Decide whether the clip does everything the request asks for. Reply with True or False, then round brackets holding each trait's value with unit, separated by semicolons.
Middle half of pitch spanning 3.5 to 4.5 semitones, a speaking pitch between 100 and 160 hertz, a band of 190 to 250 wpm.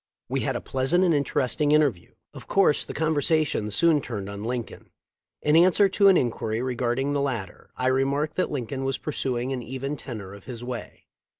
True (3.9 semitones; 135 Hz; 195 wpm)